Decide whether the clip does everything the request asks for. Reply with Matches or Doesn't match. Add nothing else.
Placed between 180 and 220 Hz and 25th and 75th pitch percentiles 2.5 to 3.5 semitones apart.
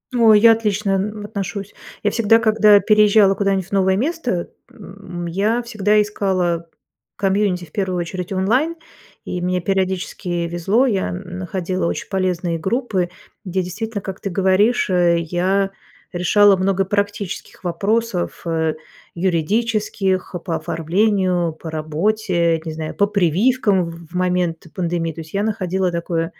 Matches